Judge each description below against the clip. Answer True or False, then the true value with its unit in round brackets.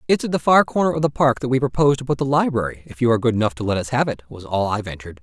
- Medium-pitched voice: False (125 Hz)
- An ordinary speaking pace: False (335 wpm)